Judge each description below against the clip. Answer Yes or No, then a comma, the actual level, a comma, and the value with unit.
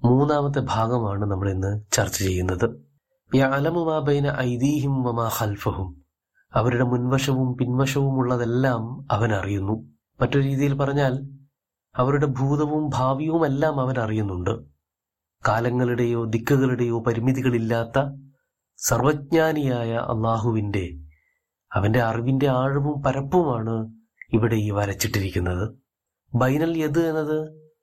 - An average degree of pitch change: Yes, average, 4.2 semitones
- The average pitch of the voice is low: Yes, low, 125 Hz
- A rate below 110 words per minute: Yes, average, 80 wpm